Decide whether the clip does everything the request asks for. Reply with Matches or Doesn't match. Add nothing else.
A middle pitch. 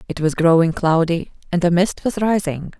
Matches